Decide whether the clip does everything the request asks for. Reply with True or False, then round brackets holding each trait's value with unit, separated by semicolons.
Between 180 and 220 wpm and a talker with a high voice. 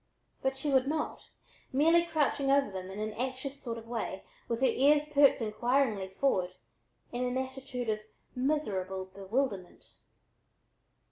False (145 wpm; 255 Hz)